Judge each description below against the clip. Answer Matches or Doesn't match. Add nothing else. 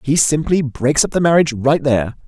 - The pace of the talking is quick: Matches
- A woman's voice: Doesn't match